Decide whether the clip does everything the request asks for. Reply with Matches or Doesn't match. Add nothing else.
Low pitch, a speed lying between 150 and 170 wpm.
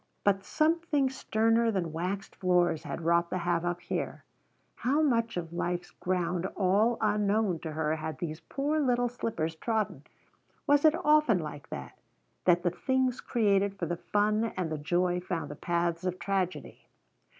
Doesn't match